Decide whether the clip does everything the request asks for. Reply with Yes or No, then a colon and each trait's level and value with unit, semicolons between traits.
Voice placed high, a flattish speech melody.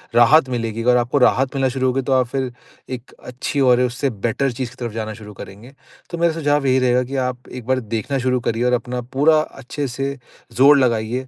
No: low, 130 Hz; narrow, 2.0 semitones